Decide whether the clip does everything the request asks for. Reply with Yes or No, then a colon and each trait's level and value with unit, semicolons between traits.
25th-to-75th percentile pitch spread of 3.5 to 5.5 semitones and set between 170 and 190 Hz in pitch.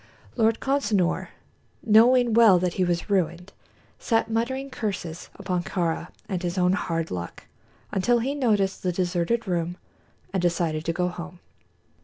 Yes: average, 4.5 semitones; medium, 185 Hz